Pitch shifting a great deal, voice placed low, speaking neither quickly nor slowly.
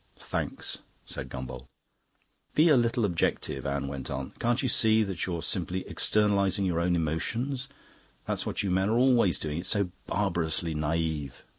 Yes: wide, 5.7 semitones; very low, 90 Hz; average, 160 wpm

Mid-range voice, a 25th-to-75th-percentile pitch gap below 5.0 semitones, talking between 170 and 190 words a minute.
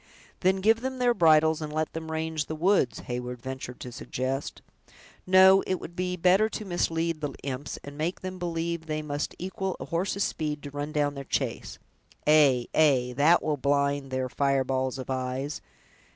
Yes: medium, 155 Hz; average, 4.2 semitones; average, 180 wpm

